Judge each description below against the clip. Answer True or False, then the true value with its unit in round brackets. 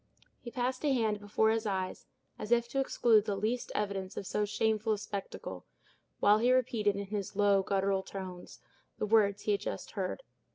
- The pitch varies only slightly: True (2.2 semitones)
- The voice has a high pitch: True (210 Hz)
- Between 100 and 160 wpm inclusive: False (190 wpm)